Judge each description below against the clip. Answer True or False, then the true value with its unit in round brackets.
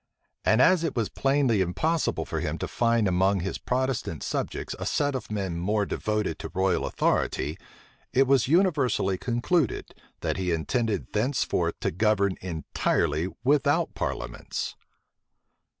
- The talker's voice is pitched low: True (110 Hz)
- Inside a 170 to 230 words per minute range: False (135 wpm)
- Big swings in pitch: True (6.3 semitones)